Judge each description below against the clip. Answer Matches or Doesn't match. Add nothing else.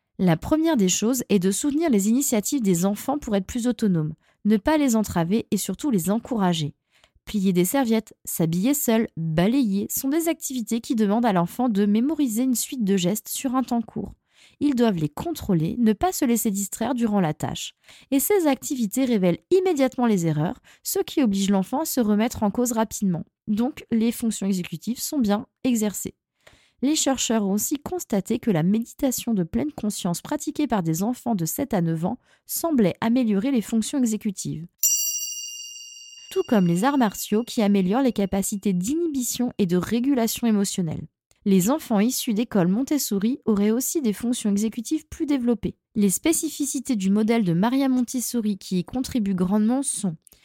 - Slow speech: Doesn't match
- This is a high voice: Matches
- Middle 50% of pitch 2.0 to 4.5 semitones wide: Doesn't match